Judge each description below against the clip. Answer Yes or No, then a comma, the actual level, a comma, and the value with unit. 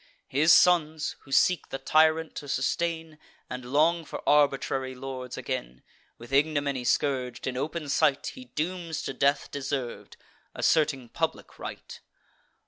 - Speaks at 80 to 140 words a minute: Yes, slow, 135 wpm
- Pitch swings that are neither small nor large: Yes, average, 3.1 semitones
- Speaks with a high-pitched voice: No, medium, 145 Hz